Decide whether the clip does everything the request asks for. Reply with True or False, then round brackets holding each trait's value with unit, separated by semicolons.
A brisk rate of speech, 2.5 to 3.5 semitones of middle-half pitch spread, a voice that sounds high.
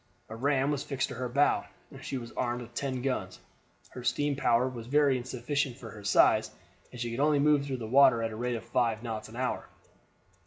False (225 wpm; 2.8 semitones; 125 Hz)